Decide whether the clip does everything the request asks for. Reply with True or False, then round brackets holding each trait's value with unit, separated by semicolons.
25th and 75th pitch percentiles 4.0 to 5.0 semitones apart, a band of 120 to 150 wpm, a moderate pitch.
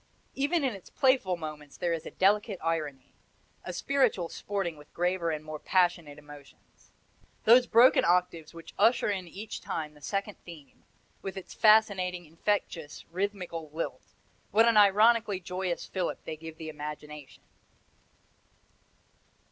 True (4.7 semitones; 135 wpm; 180 Hz)